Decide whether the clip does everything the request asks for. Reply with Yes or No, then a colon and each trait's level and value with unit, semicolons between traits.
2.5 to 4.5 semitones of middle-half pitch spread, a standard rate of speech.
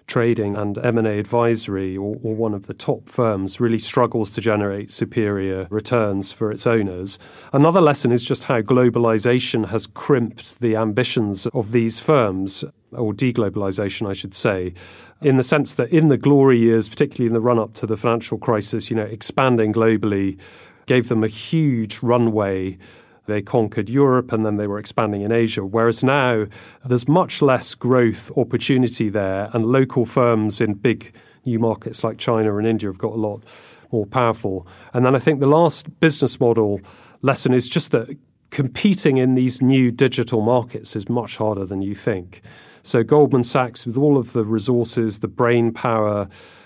Yes: average, 2.9 semitones; average, 170 wpm